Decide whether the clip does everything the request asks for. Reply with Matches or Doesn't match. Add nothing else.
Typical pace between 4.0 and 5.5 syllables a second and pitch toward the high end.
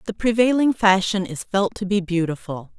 Matches